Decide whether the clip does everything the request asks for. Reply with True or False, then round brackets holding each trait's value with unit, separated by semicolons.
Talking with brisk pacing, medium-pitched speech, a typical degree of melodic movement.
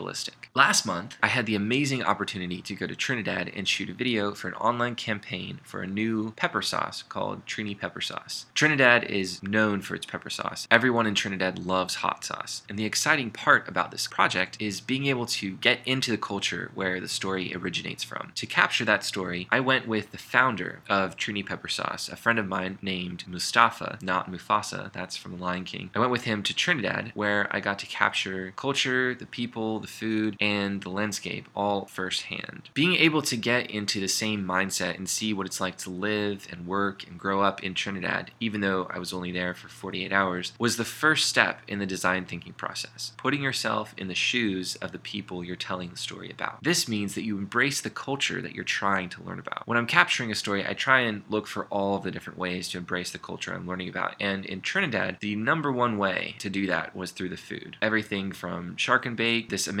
False (215 wpm; 100 Hz; 3.7 semitones)